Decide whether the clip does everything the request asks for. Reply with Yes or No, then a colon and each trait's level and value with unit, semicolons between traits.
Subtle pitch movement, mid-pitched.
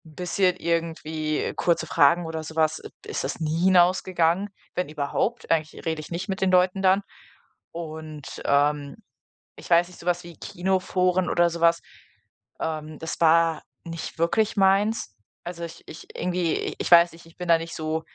Yes: narrow, 2.2 semitones; medium, 170 Hz